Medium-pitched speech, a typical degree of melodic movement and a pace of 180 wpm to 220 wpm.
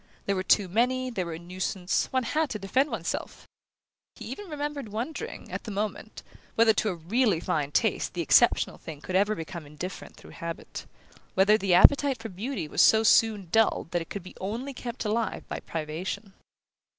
No: high, 205 Hz; average, 4.9 semitones; average, 190 wpm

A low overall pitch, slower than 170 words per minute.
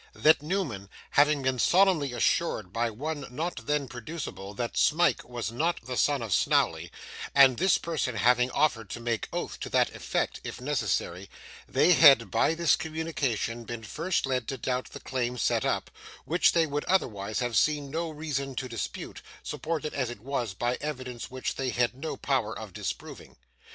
No: low, 130 Hz; average, 175 wpm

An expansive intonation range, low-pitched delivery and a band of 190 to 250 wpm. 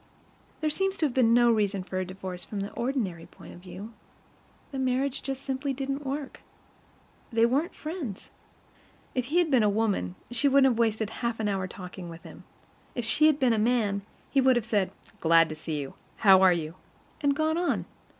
No: wide, 6.0 semitones; high, 230 Hz; average, 200 wpm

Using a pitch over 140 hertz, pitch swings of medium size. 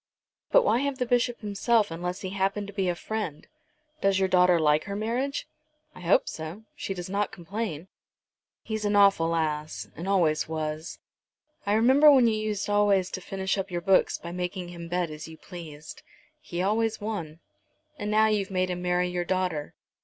Yes: high, 190 Hz; average, 3.6 semitones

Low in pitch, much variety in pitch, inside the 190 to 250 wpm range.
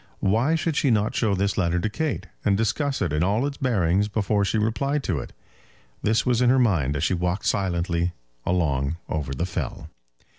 Yes: low, 100 Hz; wide, 5.7 semitones; average, 195 wpm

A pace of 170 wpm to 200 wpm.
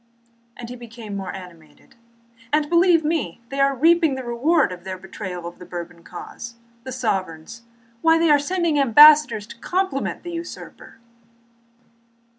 No: average, 150 wpm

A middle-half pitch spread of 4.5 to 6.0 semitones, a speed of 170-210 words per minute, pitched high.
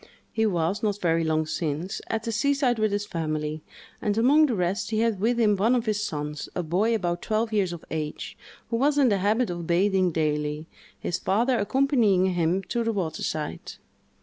Yes: average, 5.2 semitones; average, 200 wpm; high, 200 Hz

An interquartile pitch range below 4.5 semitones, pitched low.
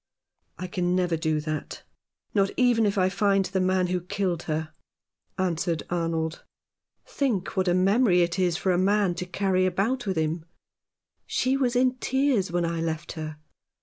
No: average, 3.0 semitones; medium, 185 Hz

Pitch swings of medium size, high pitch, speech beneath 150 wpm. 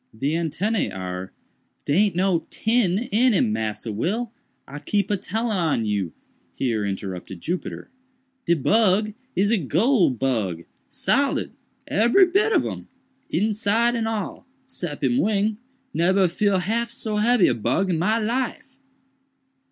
No: wide, 7.8 semitones; high, 195 Hz; average, 140 wpm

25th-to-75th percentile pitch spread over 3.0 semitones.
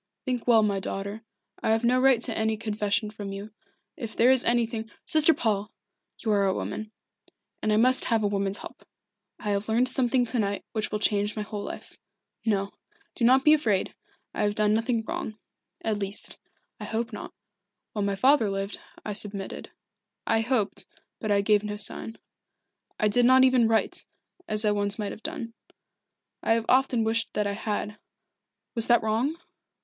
No: narrow, 2.4 semitones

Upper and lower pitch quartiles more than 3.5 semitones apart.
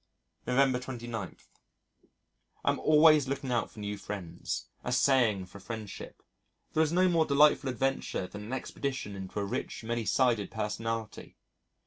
Yes: average, 4.7 semitones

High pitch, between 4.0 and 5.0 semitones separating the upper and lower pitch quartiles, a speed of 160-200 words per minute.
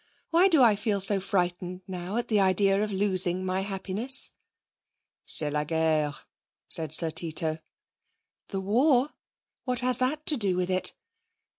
No: high, 195 Hz; average, 4.4 semitones; average, 150 wpm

